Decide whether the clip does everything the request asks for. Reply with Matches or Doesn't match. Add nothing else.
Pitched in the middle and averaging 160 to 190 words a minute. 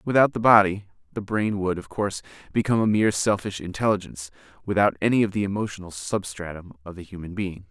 Doesn't match